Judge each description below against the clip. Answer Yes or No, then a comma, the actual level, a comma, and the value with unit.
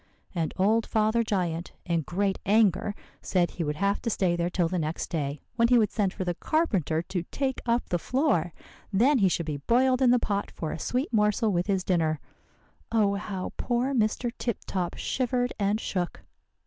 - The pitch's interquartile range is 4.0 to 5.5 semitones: Yes, average, 5.1 semitones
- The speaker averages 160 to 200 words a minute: Yes, average, 195 wpm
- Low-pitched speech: No, high, 200 Hz